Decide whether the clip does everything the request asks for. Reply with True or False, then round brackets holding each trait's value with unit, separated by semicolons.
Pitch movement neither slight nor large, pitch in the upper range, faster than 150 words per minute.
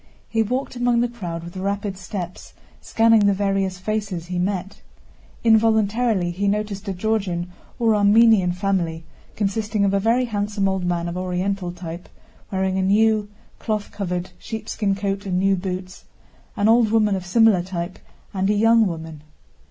True (3.1 semitones; 195 Hz; 160 wpm)